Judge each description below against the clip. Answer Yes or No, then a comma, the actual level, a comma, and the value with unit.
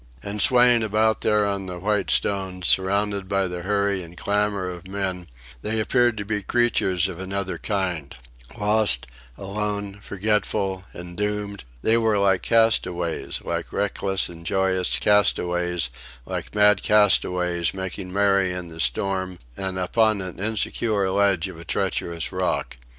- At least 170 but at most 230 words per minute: No, average, 145 wpm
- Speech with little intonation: Yes, narrow, 2.3 semitones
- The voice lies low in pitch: Yes, low, 100 Hz